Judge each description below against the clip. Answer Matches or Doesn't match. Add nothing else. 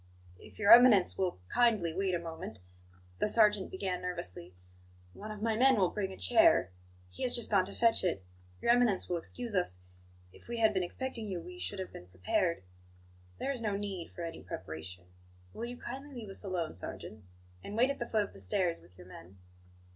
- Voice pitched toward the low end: Doesn't match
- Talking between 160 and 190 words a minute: Doesn't match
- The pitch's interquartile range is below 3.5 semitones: Doesn't match